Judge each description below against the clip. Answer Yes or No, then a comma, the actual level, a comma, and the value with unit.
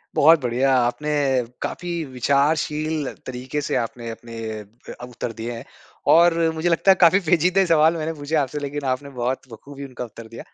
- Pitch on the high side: No, medium, 140 Hz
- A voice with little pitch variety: No, average, 4.4 semitones